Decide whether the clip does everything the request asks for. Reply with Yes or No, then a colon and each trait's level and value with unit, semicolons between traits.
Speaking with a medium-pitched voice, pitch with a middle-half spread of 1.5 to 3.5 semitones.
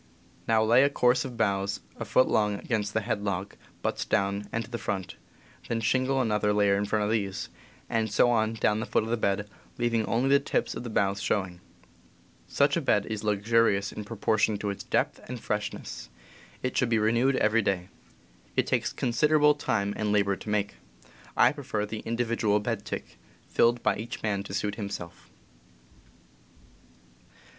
No: low, 110 Hz; narrow, 2.5 semitones